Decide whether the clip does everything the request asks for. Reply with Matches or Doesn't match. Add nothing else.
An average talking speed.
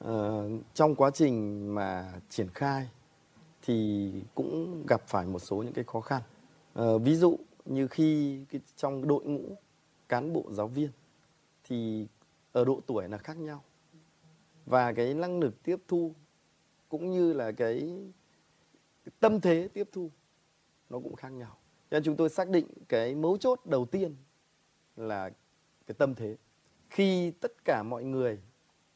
Doesn't match